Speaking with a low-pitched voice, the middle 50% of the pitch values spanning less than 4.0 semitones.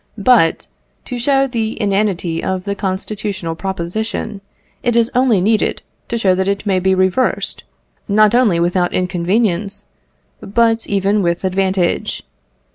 No: high, 200 Hz; average, 3.0 semitones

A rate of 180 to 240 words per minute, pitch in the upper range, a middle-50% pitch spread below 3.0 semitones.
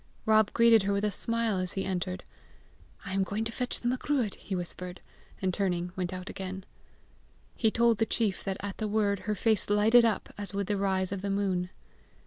Yes: fast, 205 wpm; high, 200 Hz; narrow, 2.6 semitones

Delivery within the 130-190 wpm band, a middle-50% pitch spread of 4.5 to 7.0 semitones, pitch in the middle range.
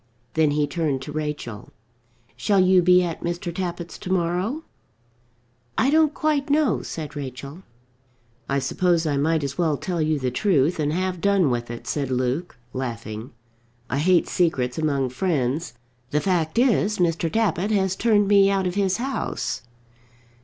Yes: average, 160 wpm; average, 5.1 semitones; medium, 170 Hz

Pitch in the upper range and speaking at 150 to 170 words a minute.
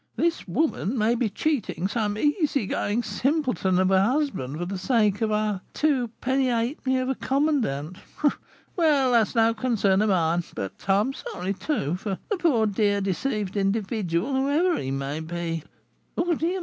Yes: high, 215 Hz; average, 165 wpm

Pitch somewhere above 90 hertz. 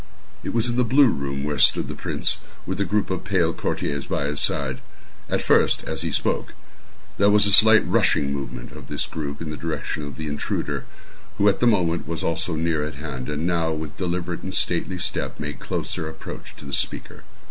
No: very low, 80 Hz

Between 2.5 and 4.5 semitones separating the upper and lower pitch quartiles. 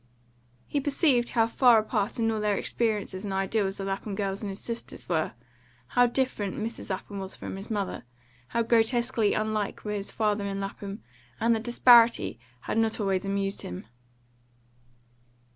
Yes: average, 2.9 semitones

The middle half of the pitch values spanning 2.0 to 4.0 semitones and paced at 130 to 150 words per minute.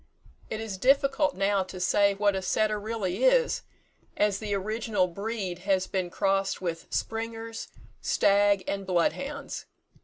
Yes: average, 2.9 semitones; average, 145 wpm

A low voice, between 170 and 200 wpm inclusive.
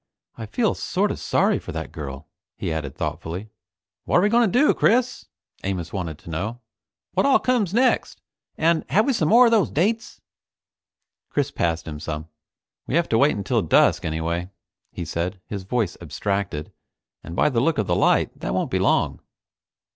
Yes: low, 105 Hz; average, 180 wpm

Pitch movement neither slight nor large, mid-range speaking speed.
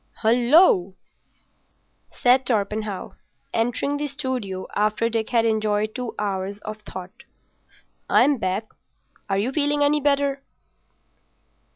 No: average, 4.8 semitones; slow, 105 wpm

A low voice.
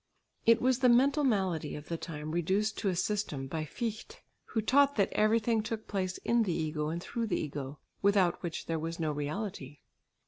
No: high, 190 Hz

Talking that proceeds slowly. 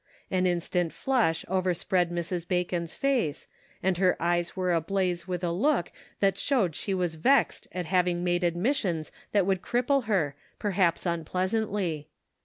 No: average, 145 wpm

